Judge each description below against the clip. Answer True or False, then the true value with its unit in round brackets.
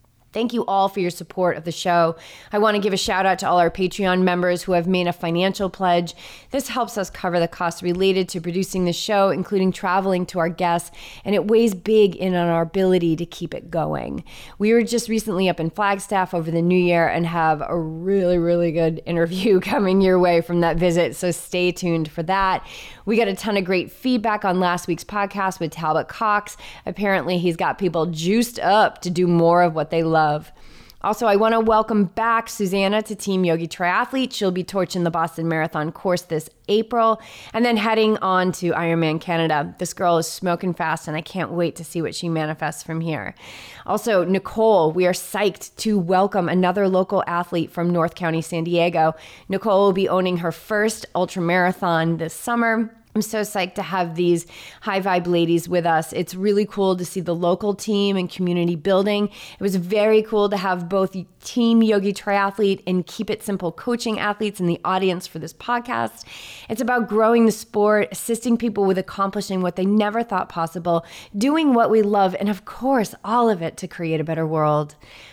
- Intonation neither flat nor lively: True (3.3 semitones)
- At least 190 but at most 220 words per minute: True (200 wpm)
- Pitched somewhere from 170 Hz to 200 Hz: True (185 Hz)